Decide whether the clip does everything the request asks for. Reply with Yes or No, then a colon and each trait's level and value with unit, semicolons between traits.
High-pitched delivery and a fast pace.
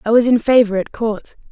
Yes: high, 225 Hz; fast, 240 wpm